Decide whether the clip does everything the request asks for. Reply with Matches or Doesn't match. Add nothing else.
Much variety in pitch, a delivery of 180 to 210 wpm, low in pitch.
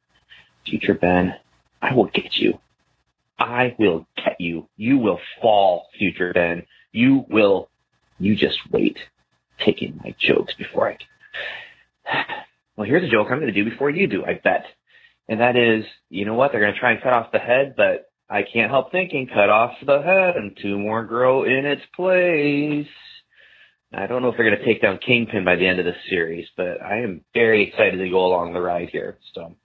Matches